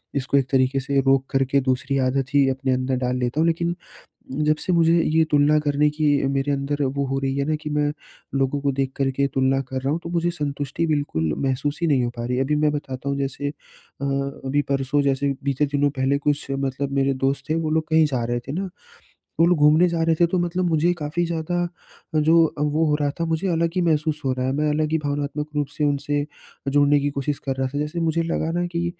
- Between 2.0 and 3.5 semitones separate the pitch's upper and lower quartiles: Yes, narrow, 2.6 semitones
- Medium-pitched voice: Yes, medium, 145 Hz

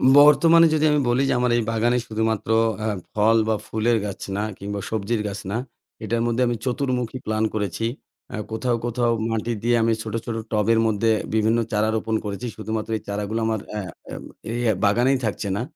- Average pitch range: No, narrow, 1.9 semitones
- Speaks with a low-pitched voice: Yes, low, 115 Hz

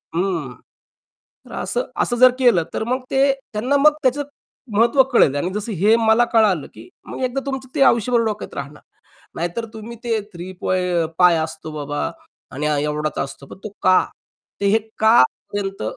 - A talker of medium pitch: No, high, 210 Hz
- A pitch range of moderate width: No, wide, 6.2 semitones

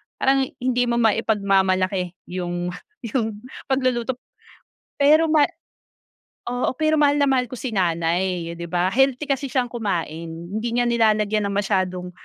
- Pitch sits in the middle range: No, high, 220 Hz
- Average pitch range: No, wide, 5.7 semitones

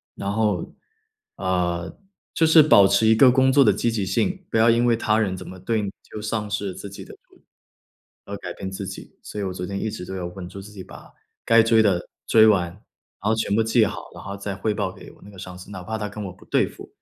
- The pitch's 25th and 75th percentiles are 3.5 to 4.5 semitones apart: No, average, 2.8 semitones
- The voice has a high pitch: No, low, 105 Hz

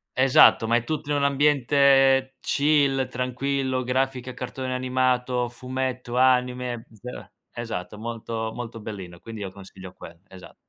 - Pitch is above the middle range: No, low, 125 Hz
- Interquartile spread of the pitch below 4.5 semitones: Yes, narrow, 2.5 semitones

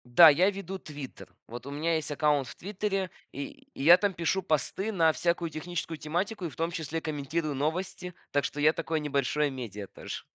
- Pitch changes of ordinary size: Yes, average, 3.3 semitones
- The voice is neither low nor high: Yes, medium, 160 Hz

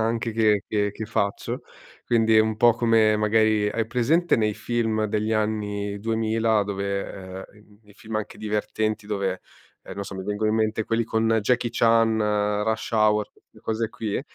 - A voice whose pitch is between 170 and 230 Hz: No, low, 110 Hz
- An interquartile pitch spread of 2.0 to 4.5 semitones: No, narrow, 1.4 semitones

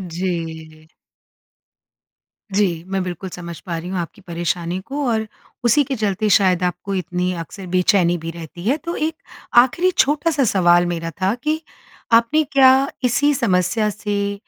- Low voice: No, high, 190 Hz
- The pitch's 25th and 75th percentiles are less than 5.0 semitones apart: No, wide, 5.5 semitones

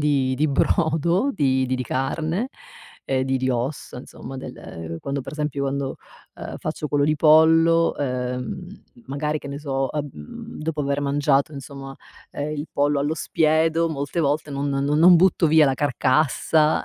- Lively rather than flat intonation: No, narrow, 2.5 semitones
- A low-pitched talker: No, medium, 145 Hz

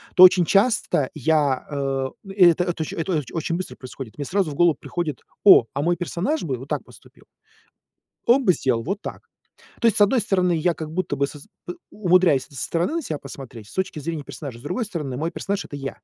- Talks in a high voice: No, medium, 165 Hz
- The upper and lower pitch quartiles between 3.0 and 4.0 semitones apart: No, average, 4.8 semitones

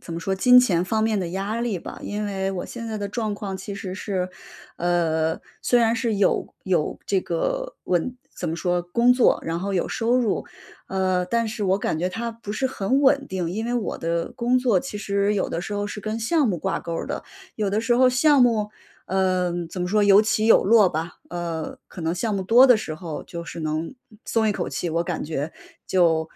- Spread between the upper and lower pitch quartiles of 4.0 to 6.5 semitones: Yes, average, 4.5 semitones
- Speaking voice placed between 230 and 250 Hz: No, high, 200 Hz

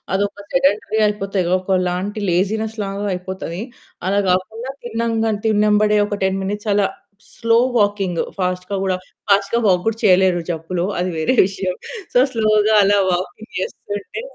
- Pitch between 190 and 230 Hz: Yes, high, 200 Hz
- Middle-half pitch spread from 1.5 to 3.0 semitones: Yes, narrow, 2.5 semitones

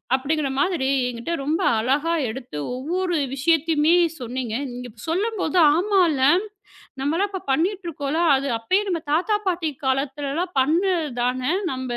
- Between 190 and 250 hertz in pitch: No, very high, 305 Hz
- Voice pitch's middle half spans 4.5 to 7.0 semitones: Yes, average, 4.9 semitones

